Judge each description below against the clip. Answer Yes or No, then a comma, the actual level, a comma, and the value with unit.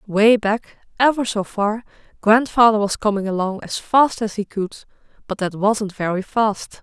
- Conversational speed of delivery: Yes, average, 165 wpm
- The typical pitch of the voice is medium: No, high, 215 Hz